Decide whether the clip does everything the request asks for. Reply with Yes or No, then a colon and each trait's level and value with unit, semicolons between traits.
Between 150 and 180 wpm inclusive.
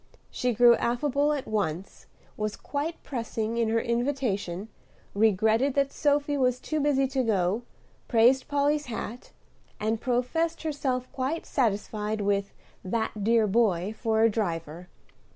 No: slow, 135 wpm